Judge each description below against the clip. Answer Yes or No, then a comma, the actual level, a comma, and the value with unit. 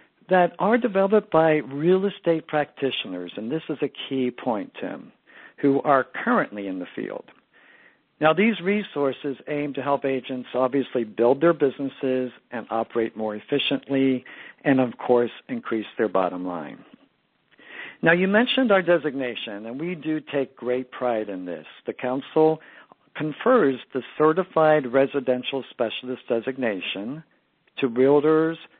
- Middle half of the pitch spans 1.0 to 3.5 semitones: No, average, 4.1 semitones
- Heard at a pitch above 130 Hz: Yes, medium, 140 Hz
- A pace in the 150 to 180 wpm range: No, slow, 135 wpm